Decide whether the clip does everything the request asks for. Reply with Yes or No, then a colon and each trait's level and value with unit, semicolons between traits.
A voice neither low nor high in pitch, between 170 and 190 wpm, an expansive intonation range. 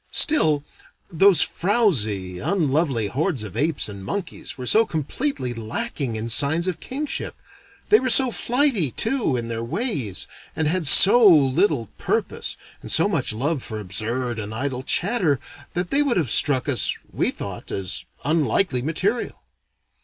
No: medium, 150 Hz; average, 150 wpm; wide, 9.0 semitones